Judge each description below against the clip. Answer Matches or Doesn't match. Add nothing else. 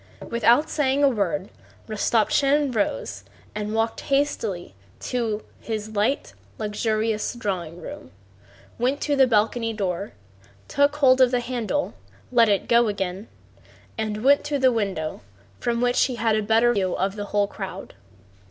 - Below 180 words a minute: Matches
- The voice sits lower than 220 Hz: Doesn't match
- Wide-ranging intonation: Doesn't match